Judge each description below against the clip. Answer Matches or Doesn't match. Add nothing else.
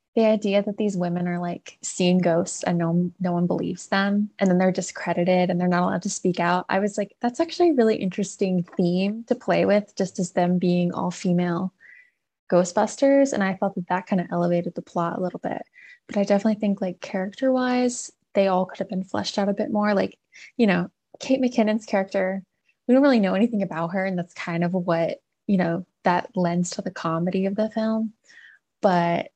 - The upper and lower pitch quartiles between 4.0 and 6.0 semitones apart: Doesn't match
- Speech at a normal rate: Doesn't match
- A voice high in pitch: Matches